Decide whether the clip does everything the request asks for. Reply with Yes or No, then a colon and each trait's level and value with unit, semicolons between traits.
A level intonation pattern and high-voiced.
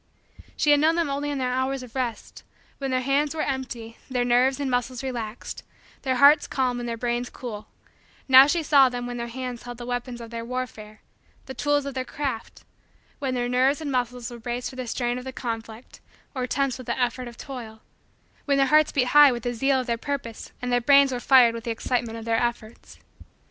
Yes: narrow, 2.2 semitones; very high, 250 Hz